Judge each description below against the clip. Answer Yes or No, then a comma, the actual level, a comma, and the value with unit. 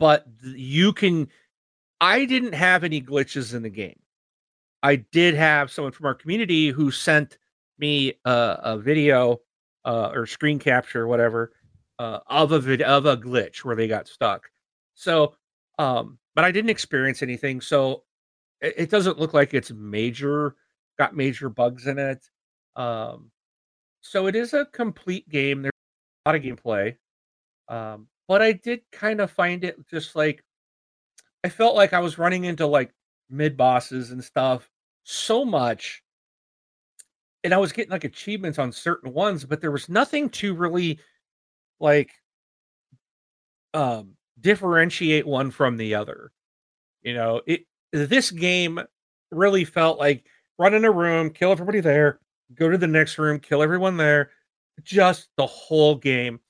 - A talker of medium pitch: Yes, medium, 150 Hz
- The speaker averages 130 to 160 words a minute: Yes, average, 155 wpm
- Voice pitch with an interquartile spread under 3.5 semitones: No, average, 5.1 semitones